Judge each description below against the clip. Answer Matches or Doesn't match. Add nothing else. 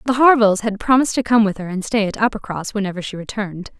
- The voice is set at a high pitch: Matches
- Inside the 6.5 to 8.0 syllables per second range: Matches